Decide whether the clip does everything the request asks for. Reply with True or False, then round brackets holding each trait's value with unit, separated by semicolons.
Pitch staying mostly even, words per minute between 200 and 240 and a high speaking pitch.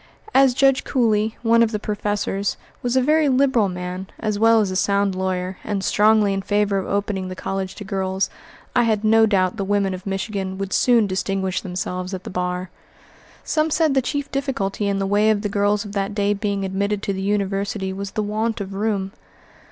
True (2.3 semitones; 205 wpm; 200 Hz)